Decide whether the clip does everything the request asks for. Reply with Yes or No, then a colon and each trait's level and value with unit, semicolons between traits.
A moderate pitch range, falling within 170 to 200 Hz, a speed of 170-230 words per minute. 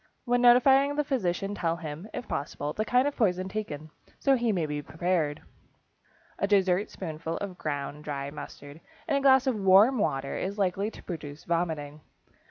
No: wide, 6.5 semitones; medium, 185 Hz; average, 175 wpm